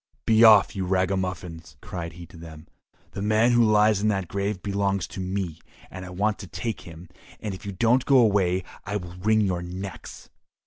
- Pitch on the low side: Yes, very low, 95 Hz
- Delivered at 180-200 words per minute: Yes, average, 190 wpm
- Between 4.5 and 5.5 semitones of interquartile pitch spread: No, average, 2.9 semitones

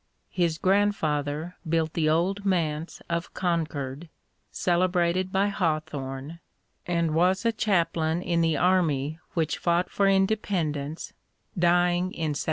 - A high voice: No, medium, 170 Hz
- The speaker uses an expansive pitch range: No, average, 2.8 semitones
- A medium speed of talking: No, slow, 120 wpm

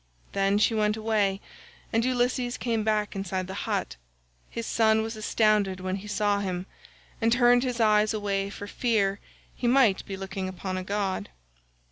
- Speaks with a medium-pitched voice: No, high, 210 Hz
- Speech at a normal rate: Yes, average, 165 wpm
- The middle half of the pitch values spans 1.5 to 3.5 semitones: Yes, narrow, 2.5 semitones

